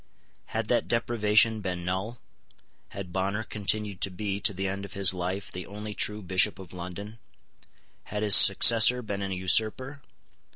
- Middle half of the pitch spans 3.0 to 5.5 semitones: No, narrow, 2.4 semitones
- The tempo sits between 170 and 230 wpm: No, average, 160 wpm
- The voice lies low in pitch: Yes, low, 100 Hz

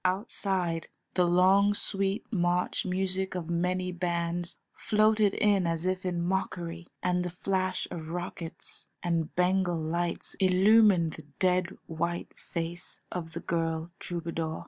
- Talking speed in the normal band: No, slow, 130 wpm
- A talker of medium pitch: Yes, medium, 180 Hz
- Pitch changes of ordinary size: No, narrow, 1.8 semitones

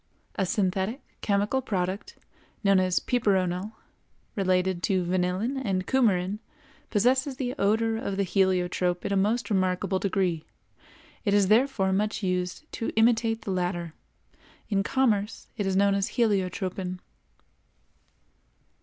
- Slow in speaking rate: Yes, slow, 125 wpm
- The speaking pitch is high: Yes, high, 195 Hz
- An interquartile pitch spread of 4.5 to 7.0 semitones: No, average, 3.2 semitones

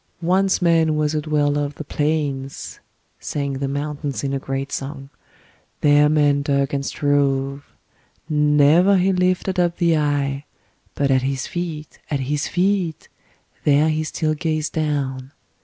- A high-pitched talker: No, medium, 150 Hz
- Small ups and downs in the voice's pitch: Yes, narrow, 2.2 semitones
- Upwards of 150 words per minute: No, average, 145 wpm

